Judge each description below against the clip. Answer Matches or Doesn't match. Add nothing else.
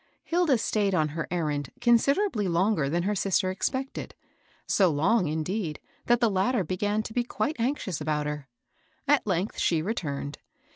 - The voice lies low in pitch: Doesn't match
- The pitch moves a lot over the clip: Matches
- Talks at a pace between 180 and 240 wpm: Doesn't match